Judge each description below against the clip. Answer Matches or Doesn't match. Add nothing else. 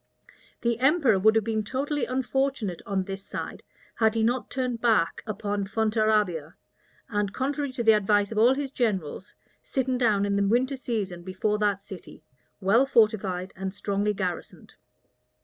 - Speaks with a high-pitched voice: Matches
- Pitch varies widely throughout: Doesn't match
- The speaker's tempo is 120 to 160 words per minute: Matches